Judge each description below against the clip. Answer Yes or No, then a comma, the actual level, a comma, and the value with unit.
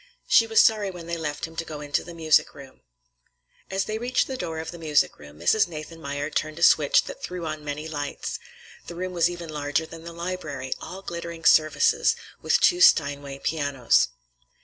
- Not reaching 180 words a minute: No, average, 195 wpm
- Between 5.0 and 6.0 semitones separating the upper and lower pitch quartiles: No, average, 3.3 semitones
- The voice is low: No, medium, 165 Hz